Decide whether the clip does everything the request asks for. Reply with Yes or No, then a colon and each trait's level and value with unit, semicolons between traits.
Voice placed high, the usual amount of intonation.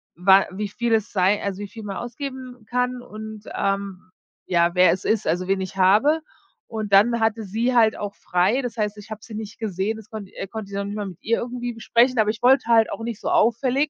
Yes: high, 215 Hz; average, 3.1 semitones